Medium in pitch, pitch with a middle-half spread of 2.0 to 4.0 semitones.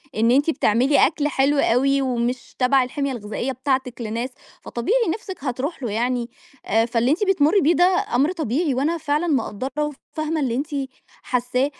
No: very high, 270 Hz; average, 3.7 semitones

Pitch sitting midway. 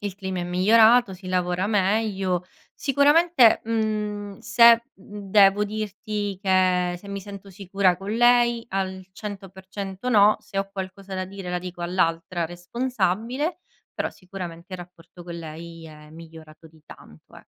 No: high, 195 Hz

